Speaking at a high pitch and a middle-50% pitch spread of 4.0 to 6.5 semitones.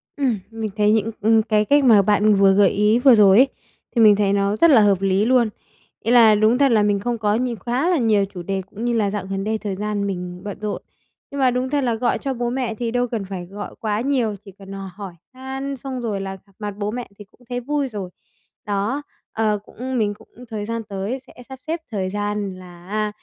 No: high, 215 Hz; average, 3.4 semitones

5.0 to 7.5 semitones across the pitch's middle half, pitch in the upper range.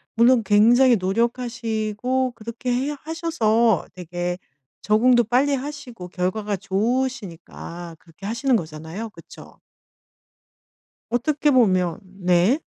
Yes: average, 5.3 semitones; high, 225 Hz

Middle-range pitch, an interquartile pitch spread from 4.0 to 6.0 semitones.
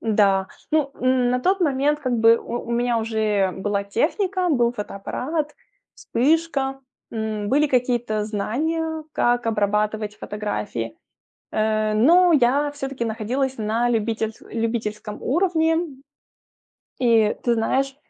No: high, 240 Hz; average, 4.5 semitones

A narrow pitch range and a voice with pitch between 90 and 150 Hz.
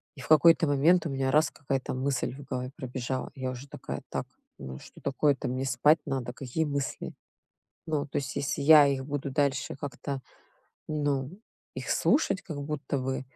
Yes: narrow, 1.9 semitones; medium, 140 Hz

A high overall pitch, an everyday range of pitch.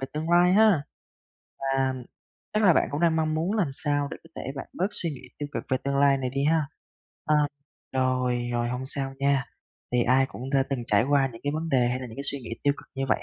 No: medium, 140 Hz; average, 3.1 semitones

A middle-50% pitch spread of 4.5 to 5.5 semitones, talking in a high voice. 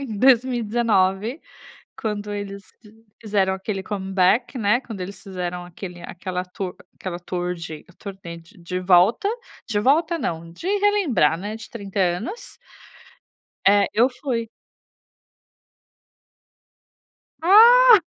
Yes: average, 4.9 semitones; high, 205 Hz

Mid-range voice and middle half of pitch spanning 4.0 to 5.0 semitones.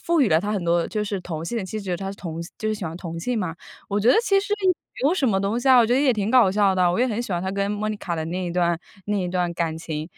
No: high, 200 Hz; average, 4.6 semitones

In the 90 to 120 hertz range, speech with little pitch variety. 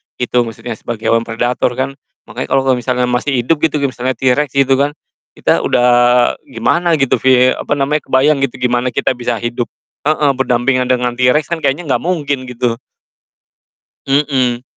No: low, 130 Hz; narrow, 2.3 semitones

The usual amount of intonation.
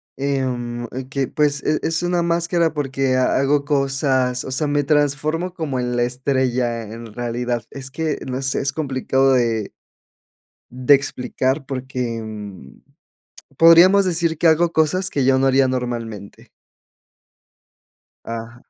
Yes: average, 3.5 semitones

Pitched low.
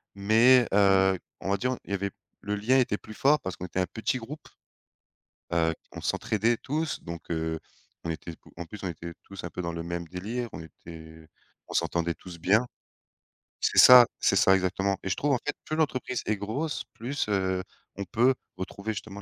Yes: low, 100 Hz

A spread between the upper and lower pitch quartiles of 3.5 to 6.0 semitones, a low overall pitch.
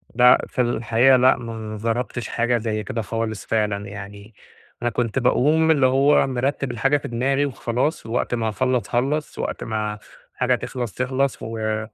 No: average, 3.0 semitones; low, 120 Hz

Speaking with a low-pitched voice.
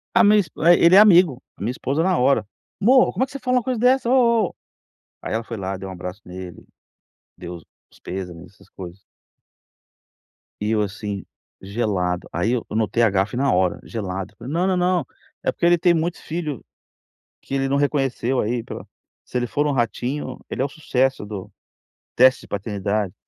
Yes: low, 125 Hz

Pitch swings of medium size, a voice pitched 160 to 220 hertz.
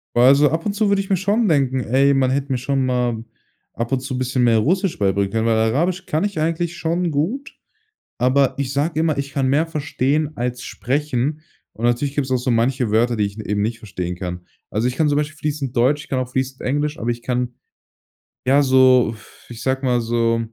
No: average, 3.9 semitones; low, 130 Hz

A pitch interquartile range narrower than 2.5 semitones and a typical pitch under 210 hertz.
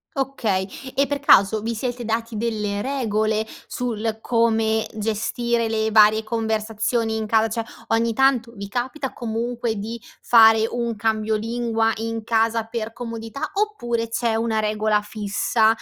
No: narrow, 1.3 semitones; high, 225 Hz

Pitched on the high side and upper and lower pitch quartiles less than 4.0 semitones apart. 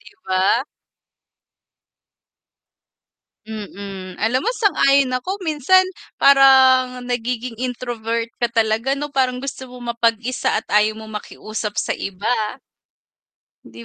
Yes: high, 245 Hz; average, 3.3 semitones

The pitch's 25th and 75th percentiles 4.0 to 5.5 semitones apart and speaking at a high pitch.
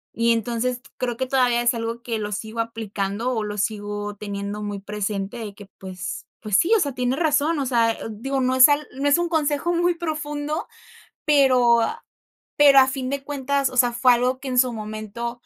Yes: average, 4.4 semitones; high, 245 Hz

